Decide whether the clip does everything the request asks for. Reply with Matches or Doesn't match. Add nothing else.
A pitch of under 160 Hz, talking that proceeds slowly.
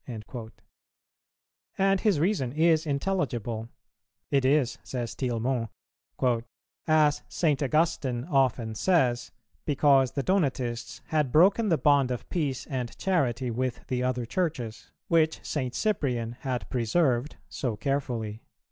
Matches